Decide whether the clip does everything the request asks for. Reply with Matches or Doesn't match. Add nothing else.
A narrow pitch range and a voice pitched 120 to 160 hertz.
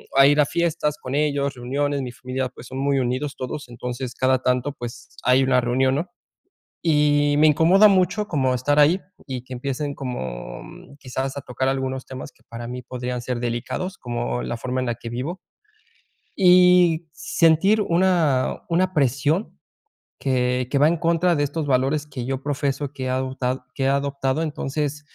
Doesn't match